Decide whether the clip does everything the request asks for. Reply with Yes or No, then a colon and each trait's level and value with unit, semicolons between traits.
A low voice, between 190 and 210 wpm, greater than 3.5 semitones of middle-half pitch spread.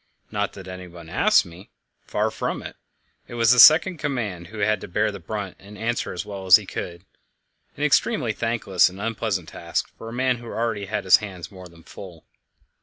Yes: low, 100 Hz; fast, 205 wpm; average, 3.9 semitones